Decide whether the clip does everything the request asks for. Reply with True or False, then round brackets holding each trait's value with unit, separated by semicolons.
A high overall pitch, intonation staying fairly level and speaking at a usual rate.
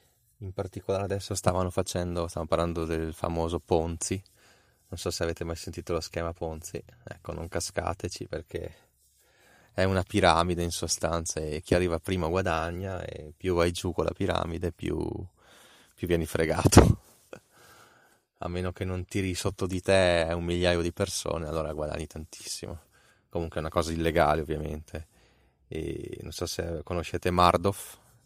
False (85 Hz; 2.1 semitones; 150 wpm)